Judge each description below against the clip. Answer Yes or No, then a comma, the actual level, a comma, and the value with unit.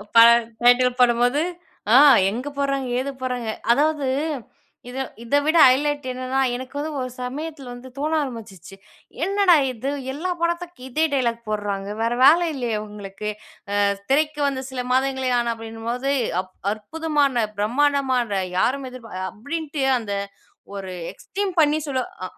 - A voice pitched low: No, very high, 260 Hz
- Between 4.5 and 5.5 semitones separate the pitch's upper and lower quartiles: No, average, 3.9 semitones